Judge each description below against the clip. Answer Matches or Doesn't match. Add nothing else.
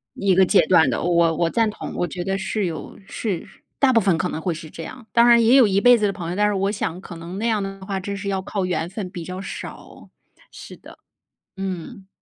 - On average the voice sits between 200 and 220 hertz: Doesn't match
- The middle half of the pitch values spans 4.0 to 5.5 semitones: Doesn't match